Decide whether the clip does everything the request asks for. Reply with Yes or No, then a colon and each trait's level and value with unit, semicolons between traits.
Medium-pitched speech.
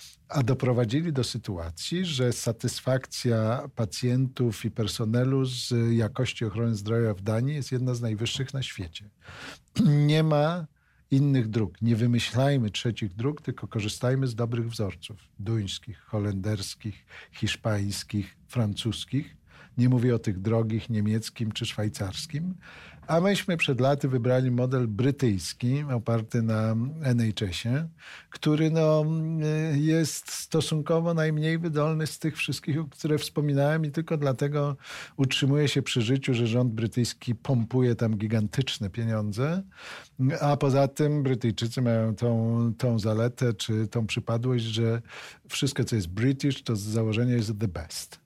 No: low, 125 Hz